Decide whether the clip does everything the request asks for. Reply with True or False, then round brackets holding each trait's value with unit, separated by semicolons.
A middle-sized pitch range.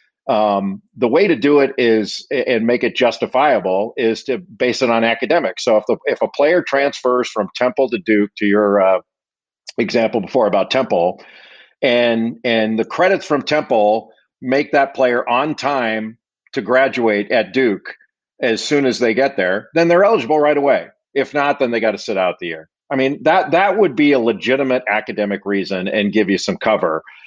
True (4.5 semitones)